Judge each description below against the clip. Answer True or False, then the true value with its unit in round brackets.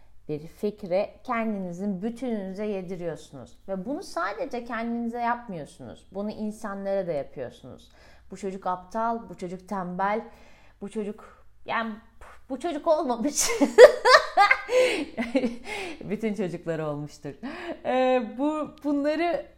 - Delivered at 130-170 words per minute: False (100 wpm)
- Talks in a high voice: True (225 Hz)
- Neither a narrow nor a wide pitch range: False (6.7 semitones)